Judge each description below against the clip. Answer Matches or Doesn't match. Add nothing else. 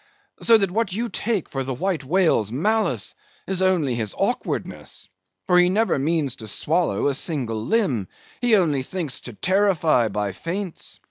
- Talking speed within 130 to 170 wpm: Matches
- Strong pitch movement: Matches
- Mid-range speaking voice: Matches